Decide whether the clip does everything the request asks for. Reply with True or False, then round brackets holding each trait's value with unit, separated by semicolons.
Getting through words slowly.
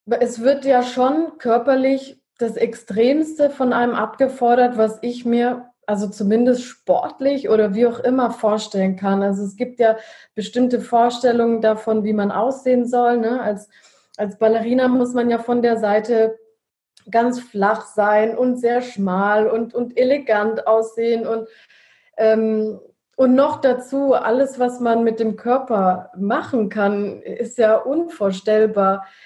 False (140 wpm)